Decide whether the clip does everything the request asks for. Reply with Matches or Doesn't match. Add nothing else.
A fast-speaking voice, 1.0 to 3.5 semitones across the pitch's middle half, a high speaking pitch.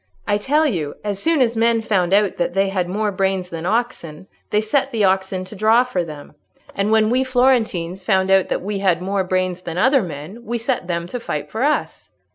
Doesn't match